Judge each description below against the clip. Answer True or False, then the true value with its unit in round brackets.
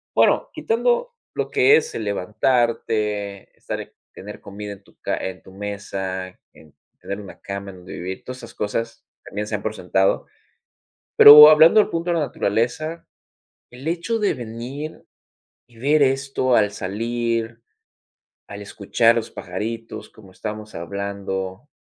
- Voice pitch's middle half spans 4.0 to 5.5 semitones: True (5.0 semitones)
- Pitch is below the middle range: True (110 Hz)